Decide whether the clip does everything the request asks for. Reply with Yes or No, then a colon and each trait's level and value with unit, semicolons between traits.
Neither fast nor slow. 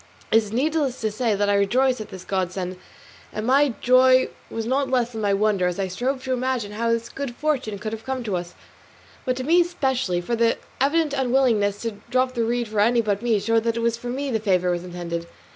No: fast, 230 wpm